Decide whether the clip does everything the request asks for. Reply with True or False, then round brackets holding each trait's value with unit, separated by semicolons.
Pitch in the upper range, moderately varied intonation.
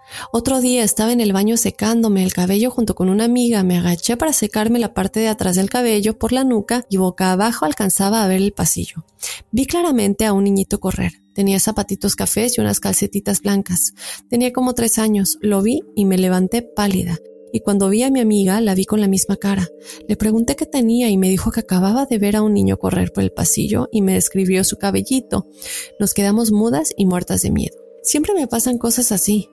True (210 Hz; 3.5 semitones)